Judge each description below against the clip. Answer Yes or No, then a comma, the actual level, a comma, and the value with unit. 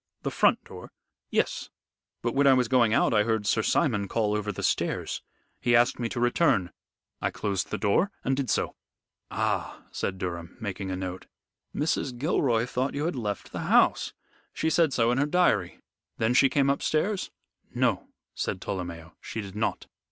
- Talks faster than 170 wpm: Yes, average, 180 wpm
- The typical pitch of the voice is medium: No, low, 115 Hz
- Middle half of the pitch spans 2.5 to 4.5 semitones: No, average, 5.3 semitones